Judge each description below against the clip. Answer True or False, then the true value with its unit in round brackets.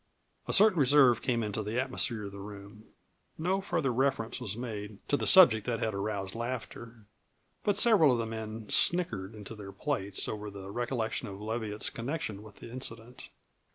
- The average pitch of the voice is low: True (115 Hz)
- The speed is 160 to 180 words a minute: True (175 wpm)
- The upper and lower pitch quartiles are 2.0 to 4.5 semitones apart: True (3.6 semitones)